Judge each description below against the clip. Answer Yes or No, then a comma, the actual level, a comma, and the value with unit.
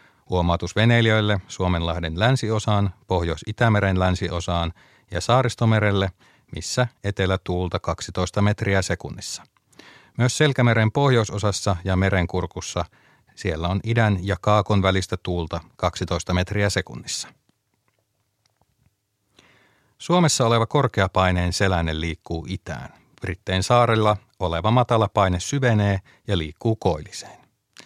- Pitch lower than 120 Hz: Yes, low, 100 Hz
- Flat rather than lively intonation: No, average, 3.7 semitones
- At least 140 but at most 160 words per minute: No, slow, 95 wpm